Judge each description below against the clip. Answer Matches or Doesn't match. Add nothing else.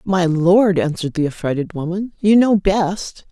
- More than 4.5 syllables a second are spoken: Doesn't match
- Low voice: Doesn't match